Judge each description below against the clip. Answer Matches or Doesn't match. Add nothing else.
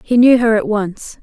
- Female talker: Matches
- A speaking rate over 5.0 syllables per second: Doesn't match